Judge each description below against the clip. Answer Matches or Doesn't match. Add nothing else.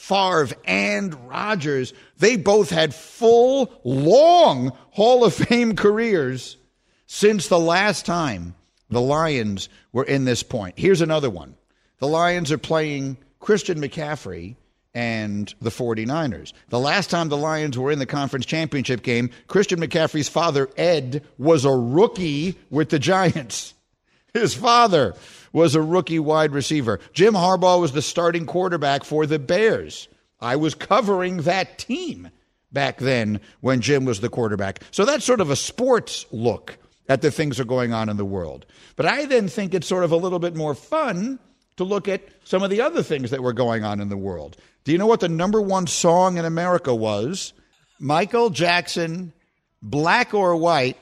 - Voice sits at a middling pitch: Matches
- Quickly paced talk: Doesn't match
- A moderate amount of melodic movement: Doesn't match